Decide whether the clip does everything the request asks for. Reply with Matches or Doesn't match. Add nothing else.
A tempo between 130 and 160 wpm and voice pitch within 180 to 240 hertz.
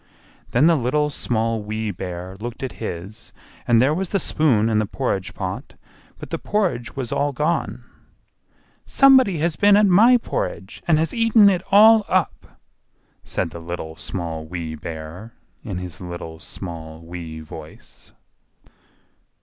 Doesn't match